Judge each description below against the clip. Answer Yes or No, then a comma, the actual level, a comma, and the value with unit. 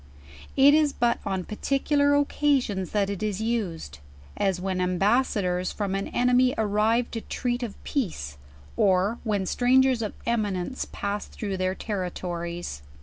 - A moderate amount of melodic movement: Yes, average, 4.7 semitones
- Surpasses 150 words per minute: No, average, 145 wpm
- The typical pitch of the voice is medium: No, high, 210 Hz